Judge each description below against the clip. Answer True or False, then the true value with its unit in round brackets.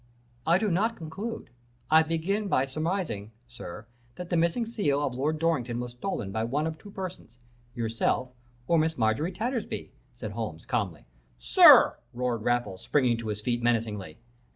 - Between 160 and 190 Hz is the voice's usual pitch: False (130 Hz)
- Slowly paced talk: False (160 wpm)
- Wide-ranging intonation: True (6.6 semitones)